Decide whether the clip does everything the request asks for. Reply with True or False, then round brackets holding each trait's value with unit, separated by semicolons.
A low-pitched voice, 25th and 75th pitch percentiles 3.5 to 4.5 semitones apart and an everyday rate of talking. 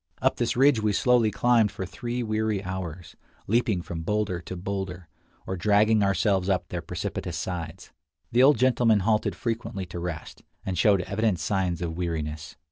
True (100 Hz; 3.8 semitones; 165 wpm)